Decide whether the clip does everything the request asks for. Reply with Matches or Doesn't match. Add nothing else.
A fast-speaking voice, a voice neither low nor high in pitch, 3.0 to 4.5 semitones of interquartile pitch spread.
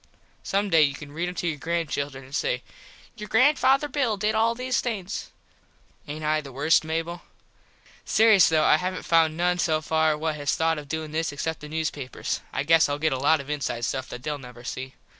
Matches